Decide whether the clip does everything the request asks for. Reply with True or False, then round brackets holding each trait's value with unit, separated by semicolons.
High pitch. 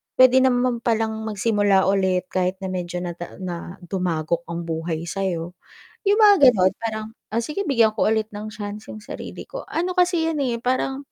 True (215 Hz)